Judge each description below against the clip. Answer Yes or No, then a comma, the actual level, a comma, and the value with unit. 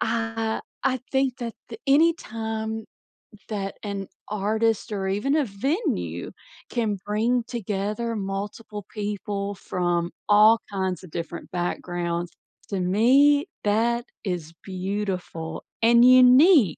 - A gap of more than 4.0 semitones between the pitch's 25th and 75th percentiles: No, average, 3.5 semitones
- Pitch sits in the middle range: No, high, 210 Hz